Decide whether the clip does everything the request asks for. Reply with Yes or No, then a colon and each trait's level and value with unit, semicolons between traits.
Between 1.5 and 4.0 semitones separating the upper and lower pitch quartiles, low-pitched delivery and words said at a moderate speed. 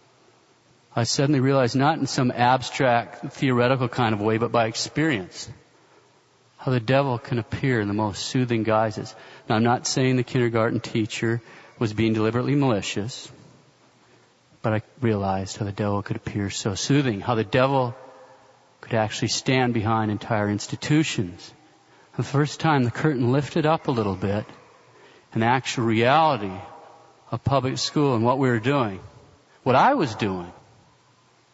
Yes: average, 3.5 semitones; low, 120 Hz; average, 150 wpm